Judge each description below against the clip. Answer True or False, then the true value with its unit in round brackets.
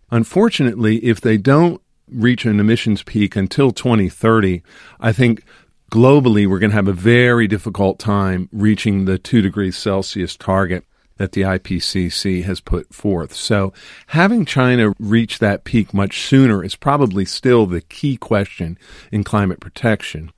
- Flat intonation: False (3.4 semitones)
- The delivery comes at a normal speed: True (145 wpm)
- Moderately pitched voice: False (105 Hz)